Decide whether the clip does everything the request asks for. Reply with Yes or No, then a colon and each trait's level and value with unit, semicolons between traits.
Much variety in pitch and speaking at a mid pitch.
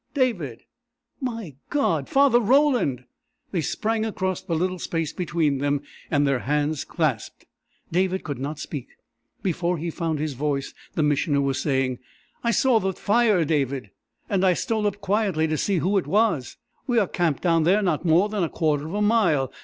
Yes: wide, 6.1 semitones; medium, 170 Hz